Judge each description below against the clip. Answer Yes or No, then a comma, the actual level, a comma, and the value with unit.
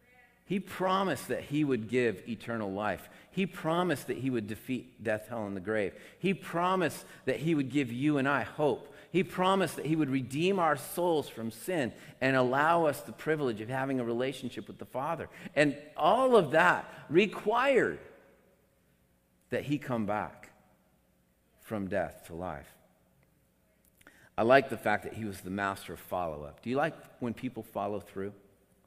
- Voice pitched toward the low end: Yes, low, 130 Hz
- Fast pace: No, average, 175 wpm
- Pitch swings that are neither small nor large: No, wide, 6.6 semitones